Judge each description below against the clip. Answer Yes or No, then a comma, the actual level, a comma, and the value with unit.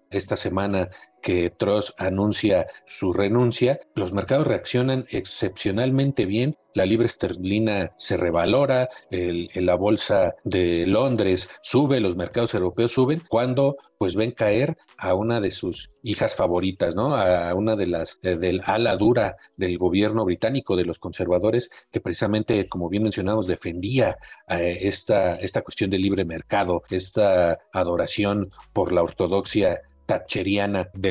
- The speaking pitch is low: Yes, low, 100 Hz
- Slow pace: No, average, 140 wpm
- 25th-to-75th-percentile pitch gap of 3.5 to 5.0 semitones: Yes, average, 4.2 semitones